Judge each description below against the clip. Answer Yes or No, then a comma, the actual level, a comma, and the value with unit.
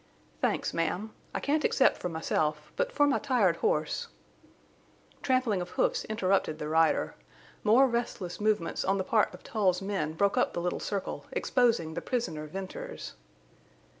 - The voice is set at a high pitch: Yes, high, 200 Hz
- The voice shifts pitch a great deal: Yes, wide, 6.3 semitones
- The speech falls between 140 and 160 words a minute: Yes, average, 150 wpm